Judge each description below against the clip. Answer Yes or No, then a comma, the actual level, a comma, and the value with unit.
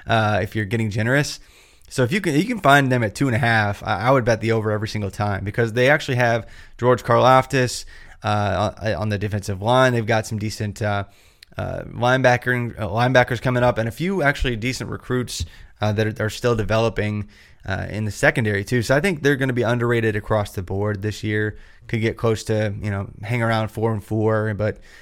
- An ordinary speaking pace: No, fast, 220 wpm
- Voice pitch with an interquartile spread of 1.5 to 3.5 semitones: Yes, average, 2.7 semitones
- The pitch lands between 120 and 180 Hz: No, low, 110 Hz